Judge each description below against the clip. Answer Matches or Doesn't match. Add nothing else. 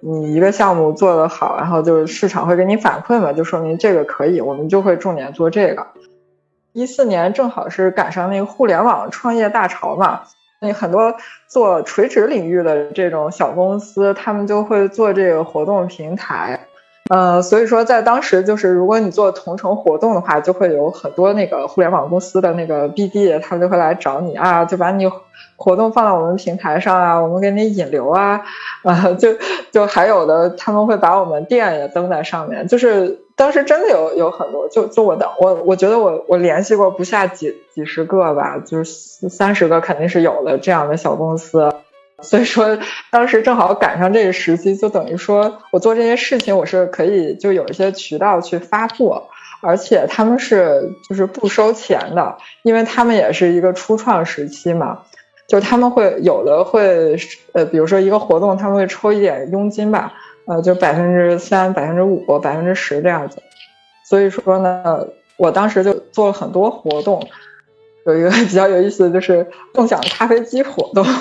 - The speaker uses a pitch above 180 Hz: Matches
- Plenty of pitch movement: Doesn't match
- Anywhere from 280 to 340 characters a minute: Matches